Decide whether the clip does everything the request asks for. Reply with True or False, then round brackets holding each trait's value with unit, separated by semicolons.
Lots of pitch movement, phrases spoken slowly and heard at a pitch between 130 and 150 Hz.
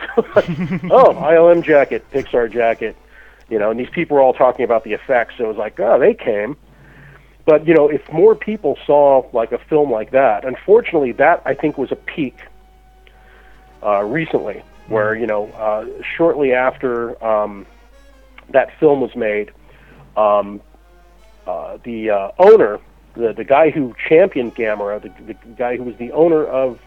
False (7.3 semitones; 170 wpm; 135 Hz)